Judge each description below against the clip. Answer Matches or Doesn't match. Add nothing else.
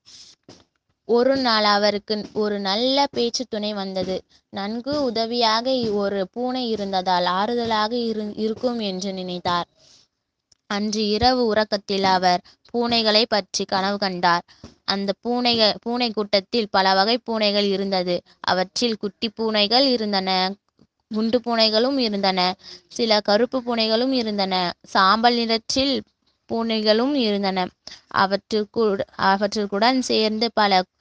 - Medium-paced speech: Matches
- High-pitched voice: Matches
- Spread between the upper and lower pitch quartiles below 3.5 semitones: Matches